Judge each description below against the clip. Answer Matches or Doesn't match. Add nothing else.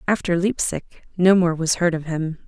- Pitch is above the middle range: Doesn't match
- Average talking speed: Matches